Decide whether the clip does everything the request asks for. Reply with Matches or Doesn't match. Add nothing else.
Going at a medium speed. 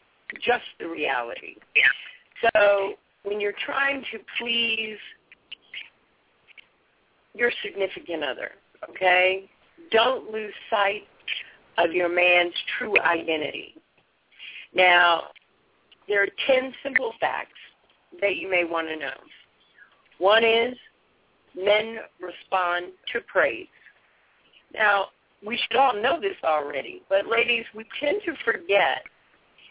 Doesn't match